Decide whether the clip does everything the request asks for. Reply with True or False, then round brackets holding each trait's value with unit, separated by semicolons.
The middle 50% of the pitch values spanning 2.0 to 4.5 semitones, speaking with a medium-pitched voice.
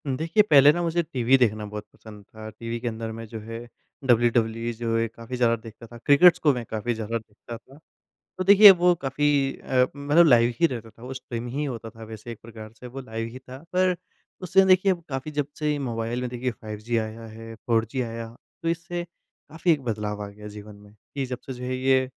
False (3.9 semitones; 120 Hz)